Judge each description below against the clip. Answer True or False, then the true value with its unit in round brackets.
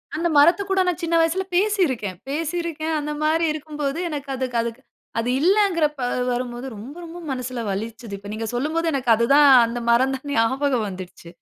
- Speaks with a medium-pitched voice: False (280 Hz)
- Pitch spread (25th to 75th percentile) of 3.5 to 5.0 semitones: False (5.5 semitones)